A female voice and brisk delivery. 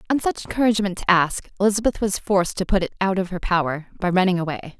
Yes: female; fast, 225 wpm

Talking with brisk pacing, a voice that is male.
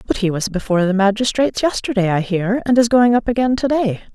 No: fast, 230 wpm; female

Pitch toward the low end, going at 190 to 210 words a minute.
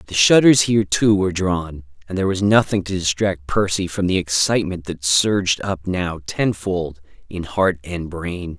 No: very low, 90 Hz; average, 175 wpm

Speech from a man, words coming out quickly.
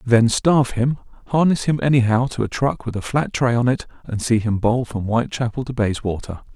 Yes: male; fast, 210 wpm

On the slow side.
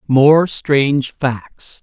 Yes: slow, 100 wpm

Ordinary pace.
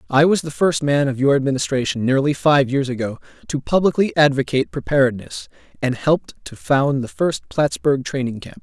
Yes: average, 175 wpm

